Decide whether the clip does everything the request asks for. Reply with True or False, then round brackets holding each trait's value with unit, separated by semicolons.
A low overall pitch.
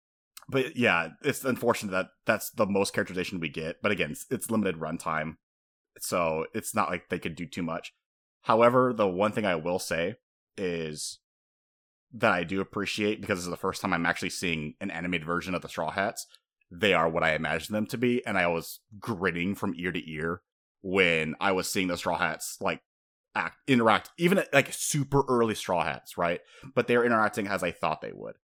True (95 Hz)